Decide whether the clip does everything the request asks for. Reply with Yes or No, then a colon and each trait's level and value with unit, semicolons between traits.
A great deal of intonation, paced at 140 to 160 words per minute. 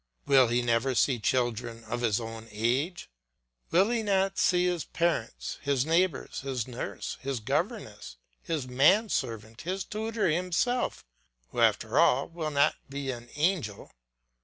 Yes: wide, 6.9 semitones; average, 145 wpm